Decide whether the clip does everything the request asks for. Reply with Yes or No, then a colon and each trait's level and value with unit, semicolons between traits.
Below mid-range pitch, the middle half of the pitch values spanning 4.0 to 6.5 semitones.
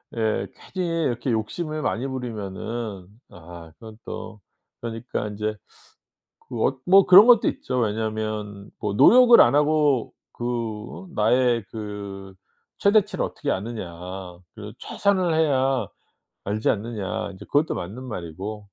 Yes: low, 115 Hz; average, 5.1 semitones